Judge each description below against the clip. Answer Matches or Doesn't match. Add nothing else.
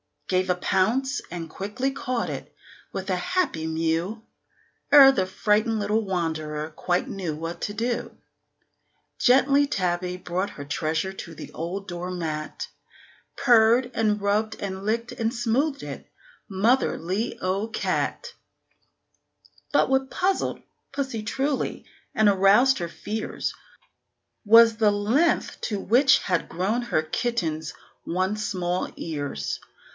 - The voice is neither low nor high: Doesn't match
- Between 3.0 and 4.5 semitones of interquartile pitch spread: Doesn't match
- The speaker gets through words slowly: Matches